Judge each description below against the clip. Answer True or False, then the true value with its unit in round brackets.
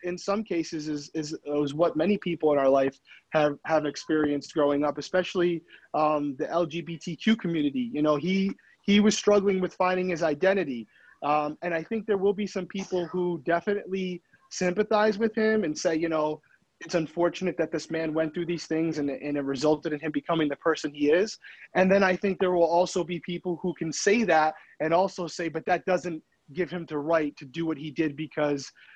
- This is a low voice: False (170 Hz)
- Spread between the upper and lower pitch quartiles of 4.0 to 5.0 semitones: False (3.1 semitones)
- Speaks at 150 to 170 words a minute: False (205 wpm)